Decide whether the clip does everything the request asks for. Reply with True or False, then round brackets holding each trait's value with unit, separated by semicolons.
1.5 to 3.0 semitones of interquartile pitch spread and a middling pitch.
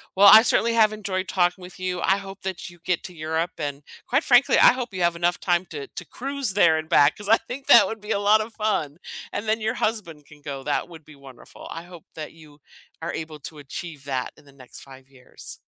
False (5.6 semitones; 175 Hz)